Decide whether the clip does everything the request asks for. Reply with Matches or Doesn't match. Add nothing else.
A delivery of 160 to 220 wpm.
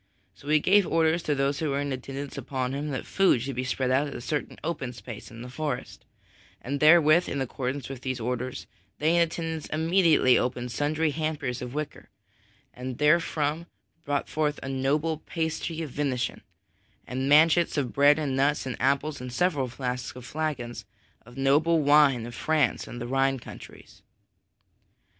Matches